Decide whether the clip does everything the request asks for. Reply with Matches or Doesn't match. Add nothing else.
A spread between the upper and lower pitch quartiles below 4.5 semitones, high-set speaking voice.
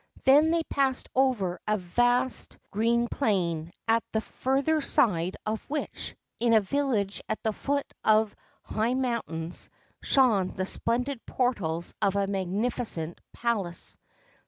Doesn't match